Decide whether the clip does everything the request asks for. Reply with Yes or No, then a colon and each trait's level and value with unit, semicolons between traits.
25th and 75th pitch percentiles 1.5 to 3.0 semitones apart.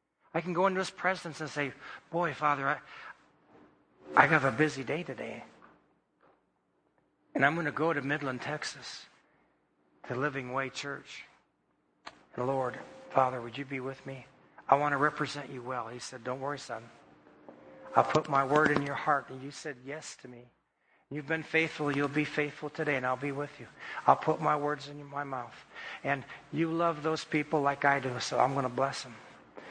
Yes: narrow, 2.4 semitones